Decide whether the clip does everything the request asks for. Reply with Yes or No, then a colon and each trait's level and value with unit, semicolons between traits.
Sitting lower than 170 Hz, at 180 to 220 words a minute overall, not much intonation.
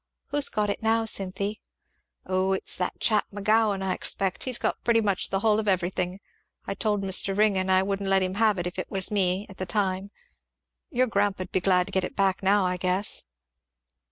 No: high, 195 Hz; fast, 205 wpm; narrow, 1.9 semitones